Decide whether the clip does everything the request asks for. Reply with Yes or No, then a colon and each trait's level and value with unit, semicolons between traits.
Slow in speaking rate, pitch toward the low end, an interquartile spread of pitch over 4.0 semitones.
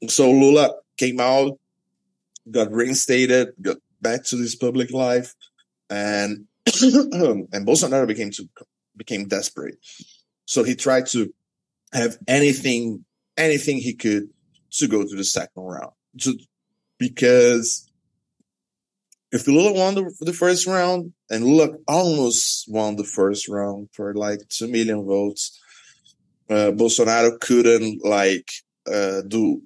Yes: slow, 120 wpm; low, 120 Hz; average, 4.4 semitones